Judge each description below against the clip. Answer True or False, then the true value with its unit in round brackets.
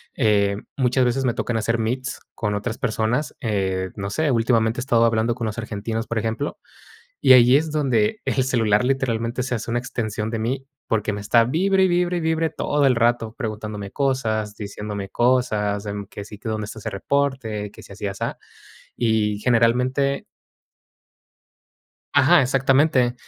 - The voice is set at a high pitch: False (115 Hz)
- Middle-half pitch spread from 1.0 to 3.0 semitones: False (3.6 semitones)